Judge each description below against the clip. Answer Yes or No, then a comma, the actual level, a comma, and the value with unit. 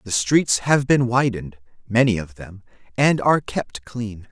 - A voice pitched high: No, low, 115 Hz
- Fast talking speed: No, average, 165 wpm